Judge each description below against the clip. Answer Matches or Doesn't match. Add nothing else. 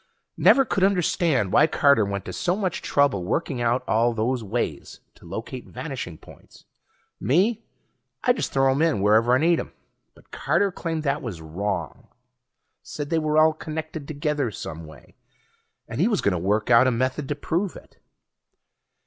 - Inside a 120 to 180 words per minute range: Matches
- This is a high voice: Doesn't match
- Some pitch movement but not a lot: Doesn't match